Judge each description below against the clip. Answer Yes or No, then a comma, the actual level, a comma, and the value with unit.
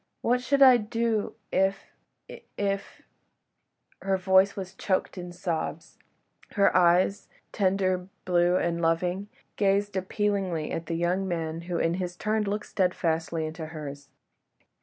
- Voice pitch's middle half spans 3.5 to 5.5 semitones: No, average, 2.7 semitones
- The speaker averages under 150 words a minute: Yes, average, 140 wpm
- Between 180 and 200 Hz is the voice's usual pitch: Yes, medium, 185 Hz